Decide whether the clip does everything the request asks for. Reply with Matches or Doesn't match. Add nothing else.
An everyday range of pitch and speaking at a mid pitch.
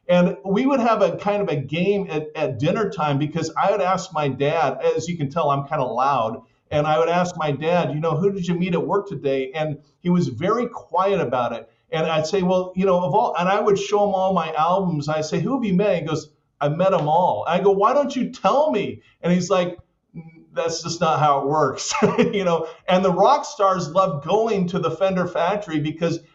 Matches